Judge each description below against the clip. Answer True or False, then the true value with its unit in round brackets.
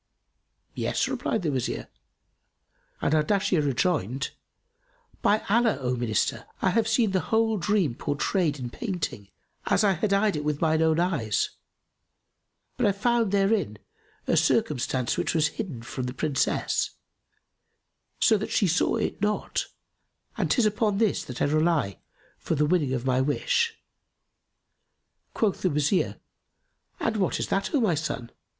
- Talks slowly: False (145 wpm)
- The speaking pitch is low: False (170 Hz)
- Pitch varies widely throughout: True (7.0 semitones)